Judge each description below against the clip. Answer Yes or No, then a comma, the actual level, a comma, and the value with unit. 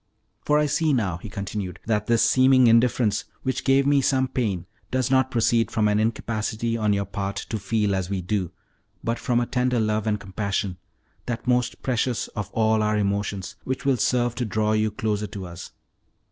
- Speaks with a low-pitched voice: Yes, low, 110 Hz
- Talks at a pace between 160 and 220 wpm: Yes, average, 190 wpm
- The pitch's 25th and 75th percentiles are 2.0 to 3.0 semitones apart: No, average, 3.4 semitones